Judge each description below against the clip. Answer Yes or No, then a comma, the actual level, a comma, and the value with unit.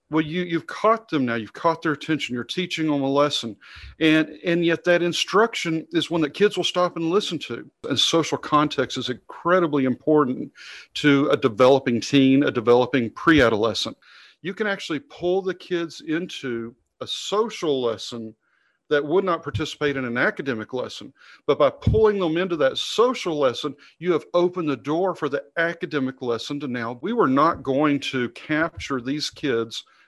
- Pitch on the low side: No, medium, 150 Hz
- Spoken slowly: No, average, 175 wpm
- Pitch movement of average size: Yes, average, 4.8 semitones